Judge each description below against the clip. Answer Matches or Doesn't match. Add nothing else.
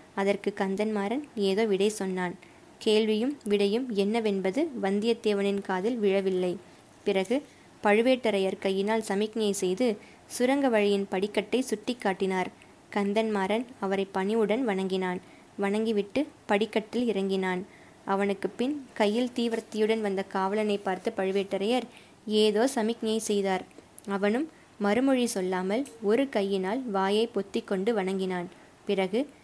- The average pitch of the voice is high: Matches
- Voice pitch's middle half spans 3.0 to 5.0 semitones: Doesn't match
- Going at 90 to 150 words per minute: Matches